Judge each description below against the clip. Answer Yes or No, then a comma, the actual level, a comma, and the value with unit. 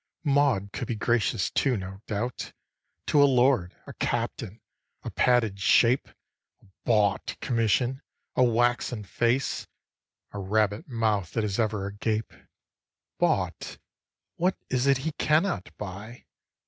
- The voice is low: Yes, low, 115 Hz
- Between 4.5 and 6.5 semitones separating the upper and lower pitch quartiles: No, average, 3.8 semitones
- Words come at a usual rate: No, slow, 125 wpm